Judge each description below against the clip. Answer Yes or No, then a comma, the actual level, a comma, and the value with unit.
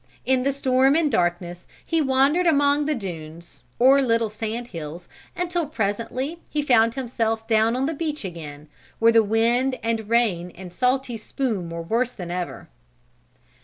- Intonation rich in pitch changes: Yes, wide, 6.3 semitones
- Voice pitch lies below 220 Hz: No, high, 230 Hz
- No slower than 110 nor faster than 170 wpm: Yes, average, 160 wpm